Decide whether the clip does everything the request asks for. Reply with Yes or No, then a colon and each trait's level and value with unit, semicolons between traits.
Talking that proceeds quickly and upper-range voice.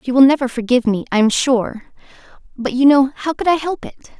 Yes: fast, 230 wpm; very high, 260 Hz